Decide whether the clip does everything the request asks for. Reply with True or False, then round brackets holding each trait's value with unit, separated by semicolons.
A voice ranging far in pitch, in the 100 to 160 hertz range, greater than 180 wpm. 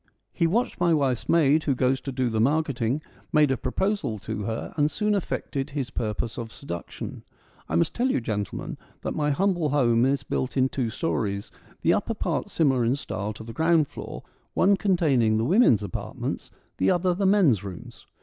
True (6.3 semitones; 135 Hz; 190 wpm)